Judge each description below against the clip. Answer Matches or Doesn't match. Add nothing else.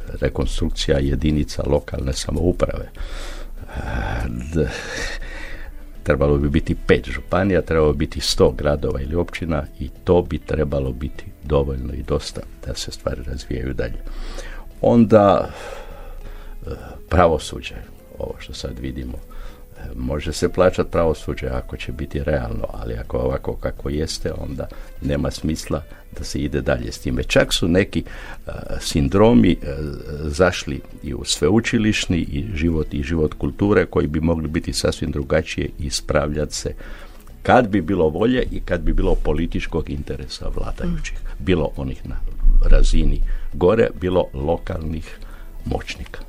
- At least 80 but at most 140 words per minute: Matches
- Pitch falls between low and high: Doesn't match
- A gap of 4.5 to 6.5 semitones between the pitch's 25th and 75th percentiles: Doesn't match